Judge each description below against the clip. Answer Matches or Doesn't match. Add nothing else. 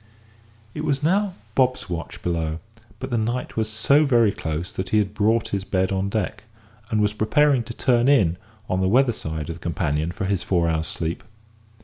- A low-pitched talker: Matches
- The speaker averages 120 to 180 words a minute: Doesn't match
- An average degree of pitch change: Doesn't match